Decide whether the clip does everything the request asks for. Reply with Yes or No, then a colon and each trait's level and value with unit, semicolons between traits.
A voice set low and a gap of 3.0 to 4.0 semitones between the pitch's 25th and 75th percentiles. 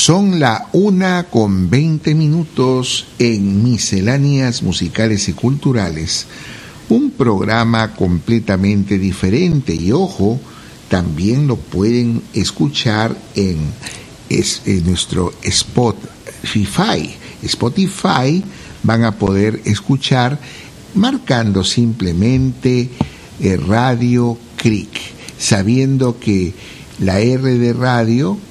No: low, 120 Hz; average, 4.8 semitones